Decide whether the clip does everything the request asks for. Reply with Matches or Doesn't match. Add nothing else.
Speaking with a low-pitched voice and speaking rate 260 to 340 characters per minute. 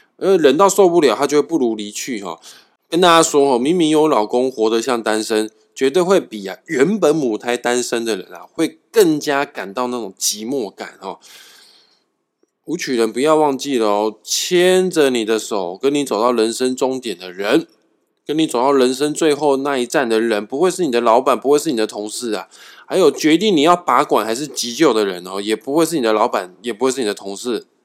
Matches